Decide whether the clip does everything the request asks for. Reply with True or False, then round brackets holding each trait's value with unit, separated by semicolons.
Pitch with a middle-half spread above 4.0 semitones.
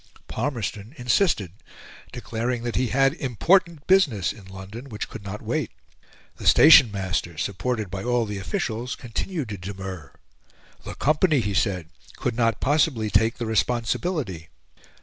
True (4.6 semitones)